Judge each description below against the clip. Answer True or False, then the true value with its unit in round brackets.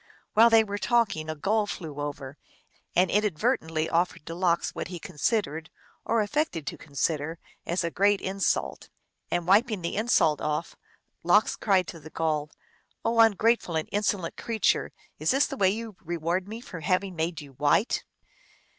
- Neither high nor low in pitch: True (180 Hz)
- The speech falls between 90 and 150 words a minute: False (165 wpm)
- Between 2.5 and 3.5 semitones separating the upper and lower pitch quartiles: False (4.7 semitones)